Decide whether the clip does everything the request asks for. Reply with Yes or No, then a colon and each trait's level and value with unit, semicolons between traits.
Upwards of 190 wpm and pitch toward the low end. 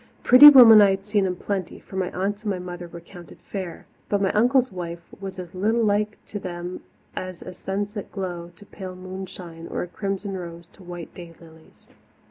No: average, 200 wpm; high, 190 Hz